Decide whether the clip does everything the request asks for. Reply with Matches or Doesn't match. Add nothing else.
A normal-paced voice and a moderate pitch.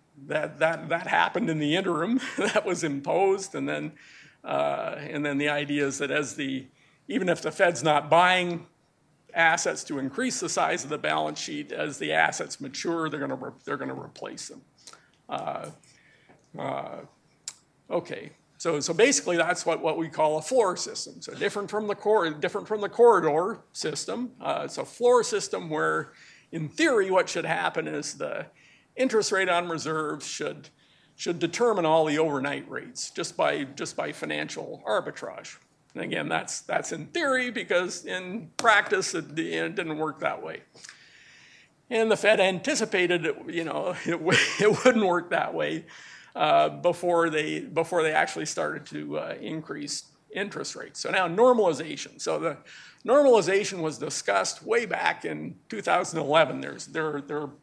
Matches